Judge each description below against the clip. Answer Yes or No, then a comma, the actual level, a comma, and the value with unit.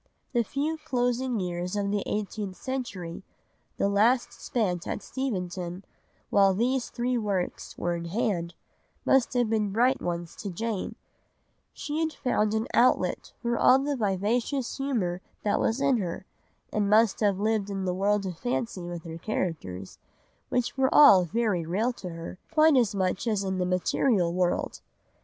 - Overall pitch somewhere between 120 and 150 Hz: No, high, 210 Hz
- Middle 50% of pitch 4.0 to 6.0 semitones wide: Yes, average, 5.0 semitones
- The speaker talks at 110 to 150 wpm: No, average, 160 wpm